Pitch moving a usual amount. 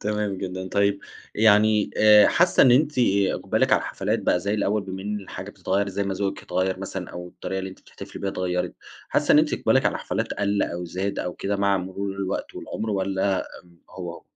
No: narrow, 1.7 semitones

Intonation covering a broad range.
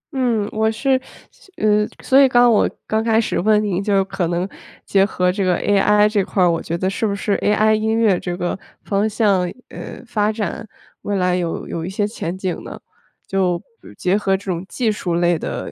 No: average, 3.0 semitones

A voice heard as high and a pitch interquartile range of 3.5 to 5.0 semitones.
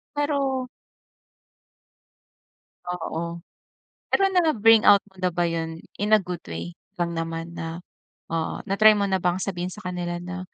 No: medium, 180 Hz; average, 3.8 semitones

